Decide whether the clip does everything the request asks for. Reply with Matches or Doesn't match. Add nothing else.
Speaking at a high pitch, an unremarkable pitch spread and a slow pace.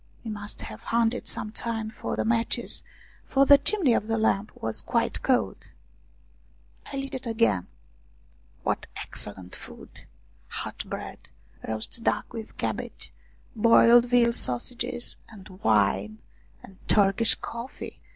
Matches